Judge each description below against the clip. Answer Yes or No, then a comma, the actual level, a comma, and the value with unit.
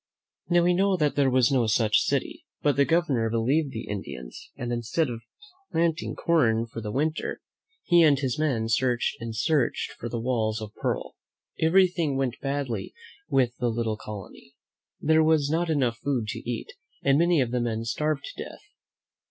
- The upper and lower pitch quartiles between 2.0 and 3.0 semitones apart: No, average, 5.3 semitones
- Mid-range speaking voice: No, low, 130 Hz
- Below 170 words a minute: No, average, 175 wpm